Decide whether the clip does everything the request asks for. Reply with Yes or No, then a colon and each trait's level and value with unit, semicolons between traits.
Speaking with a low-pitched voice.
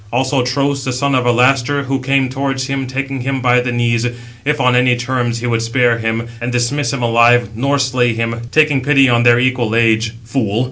Yes: low, 125 Hz